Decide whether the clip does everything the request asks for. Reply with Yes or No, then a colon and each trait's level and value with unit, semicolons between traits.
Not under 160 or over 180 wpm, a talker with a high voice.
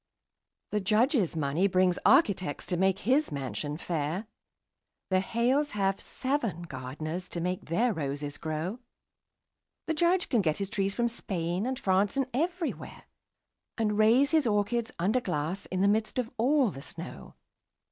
No: average, 150 wpm; high, 200 Hz